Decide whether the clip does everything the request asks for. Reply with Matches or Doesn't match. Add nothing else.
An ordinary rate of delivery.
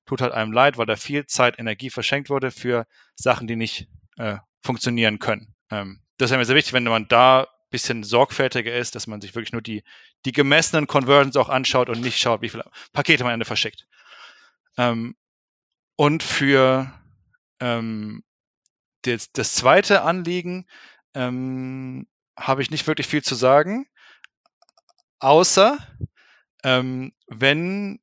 Matches